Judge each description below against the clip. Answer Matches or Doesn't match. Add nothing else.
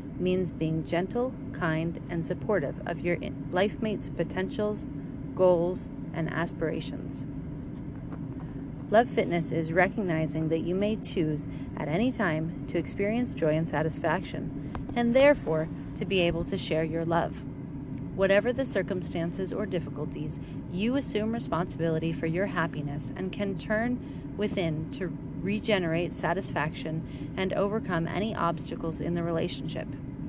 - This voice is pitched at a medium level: Matches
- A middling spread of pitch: Matches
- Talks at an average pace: Doesn't match